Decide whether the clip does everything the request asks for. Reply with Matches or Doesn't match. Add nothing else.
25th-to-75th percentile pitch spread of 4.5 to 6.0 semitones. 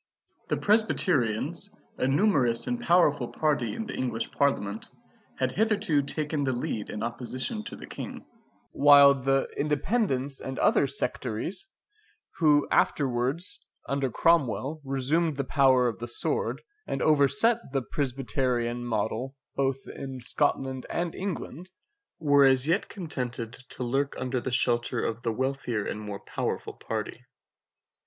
Doesn't match